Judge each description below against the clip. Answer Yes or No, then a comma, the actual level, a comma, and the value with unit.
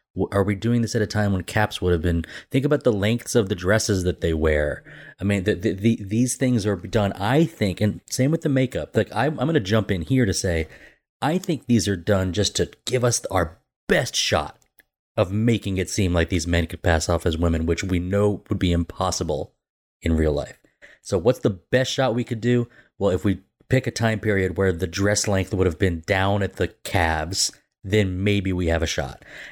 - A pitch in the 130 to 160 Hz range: No, low, 100 Hz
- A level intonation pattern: No, average, 4.3 semitones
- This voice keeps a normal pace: No, fast, 230 wpm